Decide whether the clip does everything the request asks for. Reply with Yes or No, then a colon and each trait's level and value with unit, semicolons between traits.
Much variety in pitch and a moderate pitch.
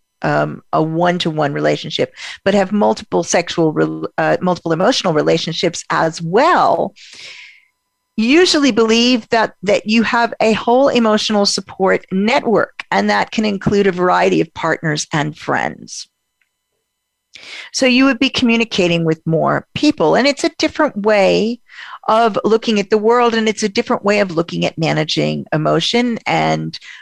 No: wide, 5.9 semitones; high, 210 Hz